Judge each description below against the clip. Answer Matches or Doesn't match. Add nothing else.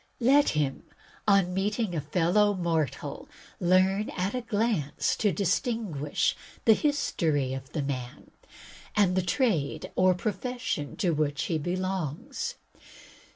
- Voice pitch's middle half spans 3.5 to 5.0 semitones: Doesn't match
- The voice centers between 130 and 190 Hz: Matches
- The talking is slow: Matches